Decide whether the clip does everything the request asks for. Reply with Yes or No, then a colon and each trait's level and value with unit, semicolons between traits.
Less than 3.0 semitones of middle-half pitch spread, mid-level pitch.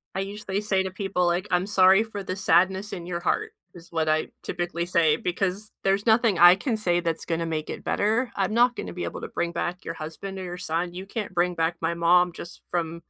Yes: narrow, 2.5 semitones; medium, 180 Hz